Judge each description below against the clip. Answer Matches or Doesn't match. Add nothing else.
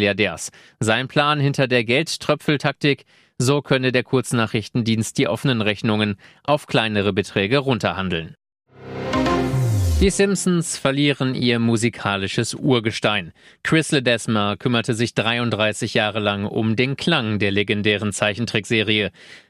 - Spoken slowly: Matches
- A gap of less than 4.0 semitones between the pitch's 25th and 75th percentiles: Doesn't match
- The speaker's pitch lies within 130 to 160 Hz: Doesn't match